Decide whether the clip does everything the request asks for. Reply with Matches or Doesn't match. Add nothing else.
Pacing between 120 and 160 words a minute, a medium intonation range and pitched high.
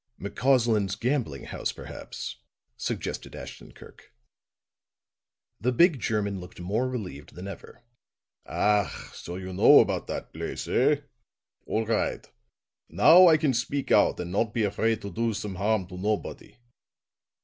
Doesn't match